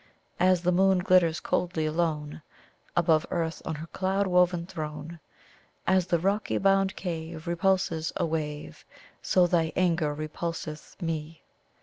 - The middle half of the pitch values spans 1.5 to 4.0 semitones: Yes, narrow, 2.6 semitones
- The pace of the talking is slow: Yes, slow, 130 wpm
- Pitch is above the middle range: No, medium, 170 Hz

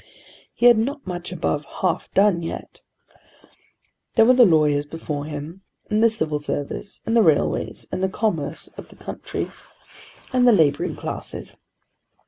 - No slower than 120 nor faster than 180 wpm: Yes, average, 150 wpm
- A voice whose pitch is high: No, medium, 180 Hz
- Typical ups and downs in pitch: No, wide, 6.7 semitones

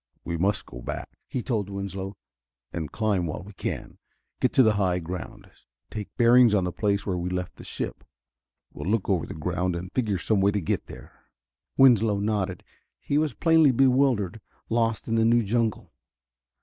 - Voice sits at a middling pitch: No, low, 100 Hz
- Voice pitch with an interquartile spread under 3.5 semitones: No, average, 4.0 semitones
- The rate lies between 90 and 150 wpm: No, average, 180 wpm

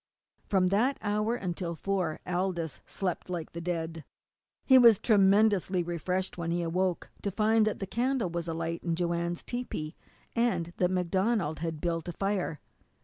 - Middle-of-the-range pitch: Yes, medium, 180 Hz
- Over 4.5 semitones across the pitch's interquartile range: No, average, 3.3 semitones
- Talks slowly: No, average, 155 wpm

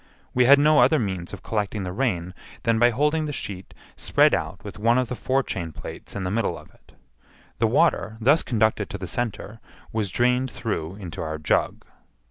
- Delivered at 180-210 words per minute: Yes, average, 195 wpm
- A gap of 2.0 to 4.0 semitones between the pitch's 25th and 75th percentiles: No, average, 4.9 semitones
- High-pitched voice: No, low, 110 Hz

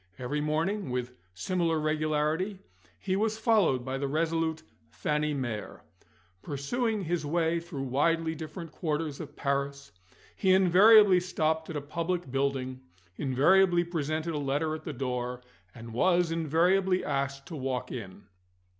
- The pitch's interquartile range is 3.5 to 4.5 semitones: Yes, average, 4.0 semitones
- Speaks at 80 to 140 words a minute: Yes, slow, 135 wpm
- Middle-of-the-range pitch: Yes, medium, 155 Hz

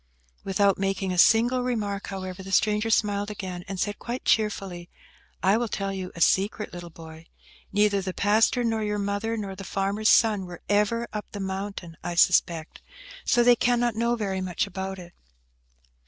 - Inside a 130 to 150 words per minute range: No, average, 175 wpm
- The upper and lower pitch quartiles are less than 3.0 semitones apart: Yes, narrow, 2.4 semitones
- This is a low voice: No, high, 200 Hz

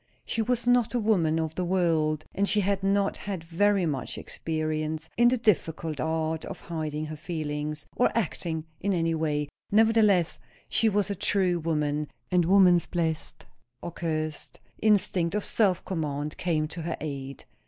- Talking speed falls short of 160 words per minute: No, average, 165 wpm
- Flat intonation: No, average, 4.3 semitones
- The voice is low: No, medium, 165 Hz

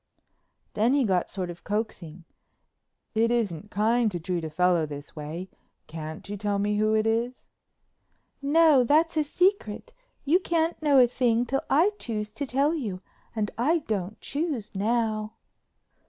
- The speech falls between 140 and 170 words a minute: Yes, average, 155 wpm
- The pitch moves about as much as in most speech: No, wide, 6.4 semitones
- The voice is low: No, high, 220 Hz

